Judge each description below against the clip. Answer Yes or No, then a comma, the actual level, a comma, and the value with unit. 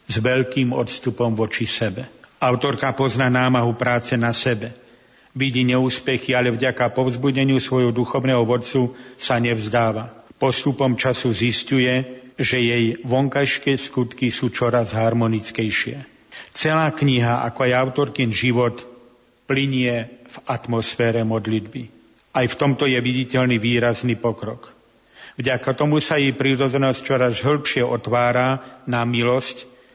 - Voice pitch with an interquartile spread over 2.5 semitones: No, narrow, 1.7 semitones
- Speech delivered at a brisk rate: No, average, 115 wpm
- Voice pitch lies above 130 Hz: No, low, 125 Hz